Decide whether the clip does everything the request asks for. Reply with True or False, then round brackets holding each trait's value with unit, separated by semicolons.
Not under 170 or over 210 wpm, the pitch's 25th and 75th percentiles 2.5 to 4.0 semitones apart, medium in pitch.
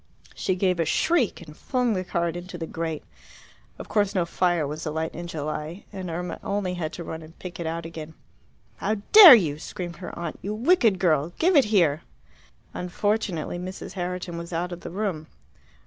True (190 wpm; 3.1 semitones; 175 Hz)